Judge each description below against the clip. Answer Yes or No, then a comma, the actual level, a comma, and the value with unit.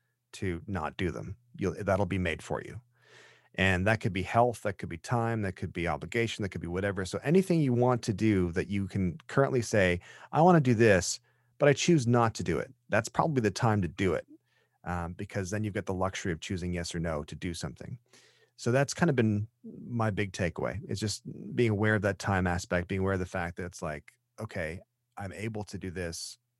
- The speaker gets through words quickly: Yes, fast, 230 wpm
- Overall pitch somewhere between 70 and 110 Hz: Yes, low, 100 Hz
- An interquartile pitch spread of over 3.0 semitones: Yes, average, 4.6 semitones